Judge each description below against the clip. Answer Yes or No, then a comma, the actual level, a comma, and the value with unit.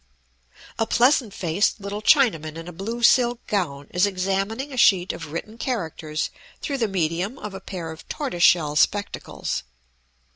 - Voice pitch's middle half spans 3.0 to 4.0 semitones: No, wide, 5.6 semitones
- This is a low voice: No, high, 195 Hz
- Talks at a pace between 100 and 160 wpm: Yes, average, 155 wpm